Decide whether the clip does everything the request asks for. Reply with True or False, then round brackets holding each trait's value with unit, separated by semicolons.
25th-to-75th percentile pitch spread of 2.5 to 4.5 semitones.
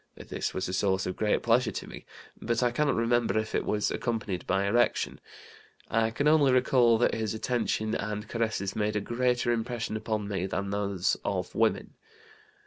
True (2.9 semitones)